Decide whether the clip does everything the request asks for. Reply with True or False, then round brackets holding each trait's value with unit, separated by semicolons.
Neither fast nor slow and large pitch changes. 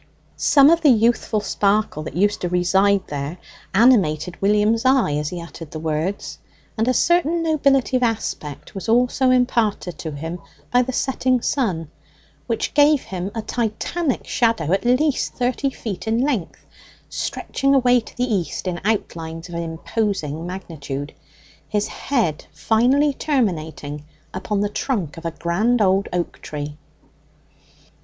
True (145 wpm; 6.8 semitones)